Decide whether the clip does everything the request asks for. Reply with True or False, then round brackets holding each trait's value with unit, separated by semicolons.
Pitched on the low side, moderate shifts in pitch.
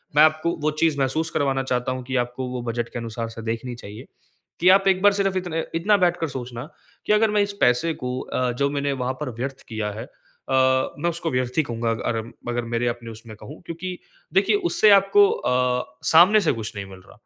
False (130 Hz; 5.9 semitones)